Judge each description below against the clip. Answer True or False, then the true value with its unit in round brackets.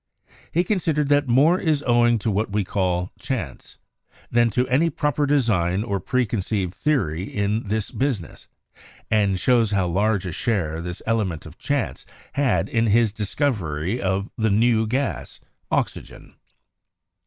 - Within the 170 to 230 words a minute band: False (145 wpm)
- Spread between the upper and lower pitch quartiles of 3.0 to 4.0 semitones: False (5.1 semitones)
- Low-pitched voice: True (110 Hz)